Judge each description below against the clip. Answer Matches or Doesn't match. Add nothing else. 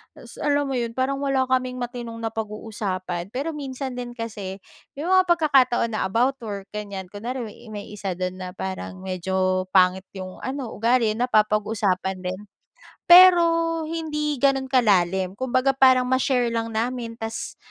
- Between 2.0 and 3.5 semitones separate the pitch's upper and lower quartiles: Doesn't match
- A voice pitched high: Matches